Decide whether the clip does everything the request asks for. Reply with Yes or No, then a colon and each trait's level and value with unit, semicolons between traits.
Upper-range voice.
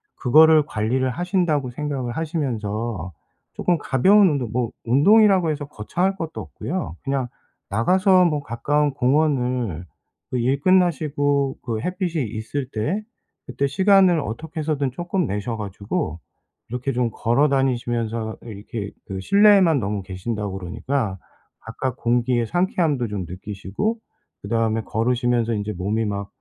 No: low, 125 Hz